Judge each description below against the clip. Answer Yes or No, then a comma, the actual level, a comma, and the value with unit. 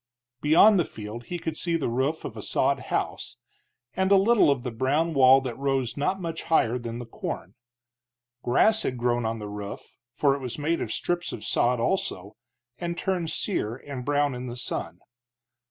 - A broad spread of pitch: Yes, wide, 5.7 semitones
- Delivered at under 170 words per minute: No, average, 190 wpm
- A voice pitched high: No, low, 135 Hz